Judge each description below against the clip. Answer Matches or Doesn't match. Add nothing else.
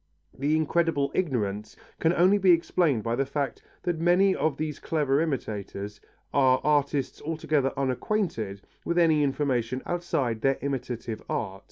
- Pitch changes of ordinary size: Matches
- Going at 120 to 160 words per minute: Matches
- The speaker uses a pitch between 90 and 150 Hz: Matches